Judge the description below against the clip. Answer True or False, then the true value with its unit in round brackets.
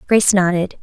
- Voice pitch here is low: False (190 Hz)